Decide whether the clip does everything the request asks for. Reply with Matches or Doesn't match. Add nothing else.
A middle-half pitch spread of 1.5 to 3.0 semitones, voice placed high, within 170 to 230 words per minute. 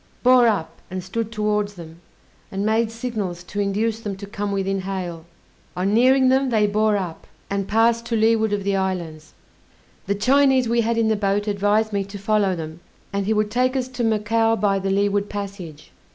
Matches